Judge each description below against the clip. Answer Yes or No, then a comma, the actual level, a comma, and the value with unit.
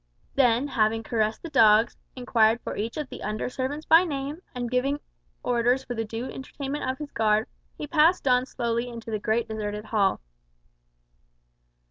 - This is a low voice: No, high, 240 Hz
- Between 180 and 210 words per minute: No, average, 165 wpm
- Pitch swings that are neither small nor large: Yes, average, 3.6 semitones